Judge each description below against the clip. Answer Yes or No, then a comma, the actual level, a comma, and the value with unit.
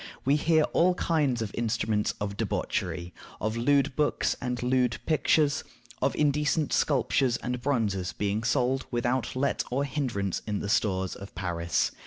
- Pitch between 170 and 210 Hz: No, low, 120 Hz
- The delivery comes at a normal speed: Yes, average, 155 wpm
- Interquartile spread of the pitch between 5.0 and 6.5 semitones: Yes, average, 5.3 semitones